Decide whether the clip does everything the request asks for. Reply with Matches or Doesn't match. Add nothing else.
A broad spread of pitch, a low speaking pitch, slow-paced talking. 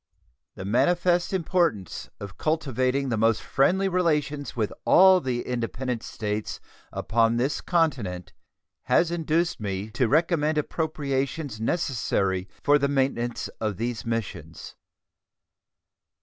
Matches